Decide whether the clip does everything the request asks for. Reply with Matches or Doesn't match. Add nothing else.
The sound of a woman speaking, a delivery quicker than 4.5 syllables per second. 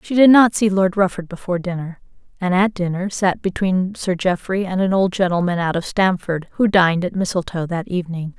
Matches